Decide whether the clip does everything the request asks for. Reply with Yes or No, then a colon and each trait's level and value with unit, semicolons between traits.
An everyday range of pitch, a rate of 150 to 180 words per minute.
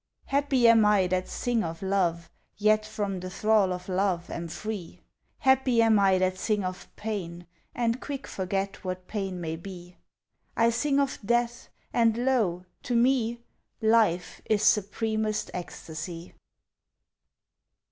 No: average, 4.0 semitones; slow, 135 wpm